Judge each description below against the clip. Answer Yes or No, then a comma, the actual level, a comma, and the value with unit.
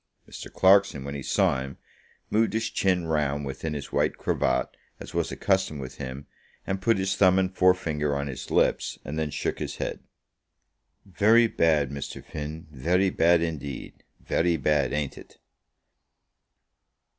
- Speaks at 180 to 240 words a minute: No, average, 155 wpm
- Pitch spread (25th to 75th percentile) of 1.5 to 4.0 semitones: No, average, 4.8 semitones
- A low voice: Yes, very low, 80 Hz